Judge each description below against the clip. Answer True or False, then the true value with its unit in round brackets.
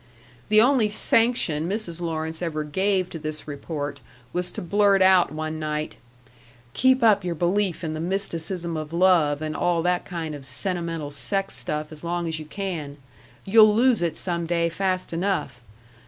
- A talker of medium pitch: True (170 Hz)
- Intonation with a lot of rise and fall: False (3.8 semitones)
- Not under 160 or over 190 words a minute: True (170 wpm)